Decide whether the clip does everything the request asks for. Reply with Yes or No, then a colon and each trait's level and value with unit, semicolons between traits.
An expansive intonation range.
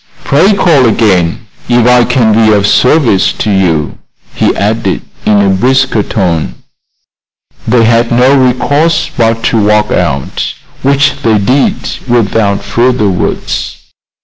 No: average, 4.1 semitones